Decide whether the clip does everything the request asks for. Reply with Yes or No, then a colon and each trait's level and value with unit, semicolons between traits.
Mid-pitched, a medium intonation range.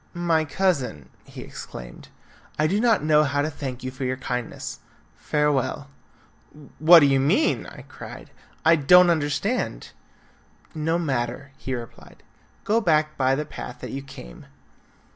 Yes: medium, 145 Hz; average, 3.6 semitones